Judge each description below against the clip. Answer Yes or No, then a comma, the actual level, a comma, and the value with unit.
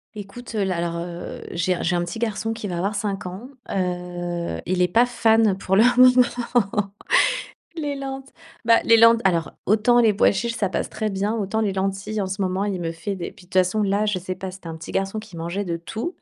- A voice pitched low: No, high, 195 Hz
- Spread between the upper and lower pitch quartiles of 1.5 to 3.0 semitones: No, average, 3.7 semitones